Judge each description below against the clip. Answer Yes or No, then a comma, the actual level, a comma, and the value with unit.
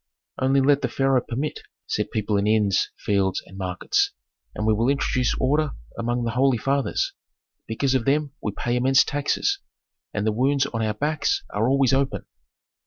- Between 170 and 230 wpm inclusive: Yes, average, 175 wpm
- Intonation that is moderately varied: Yes, average, 4.1 semitones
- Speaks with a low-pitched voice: Yes, low, 125 Hz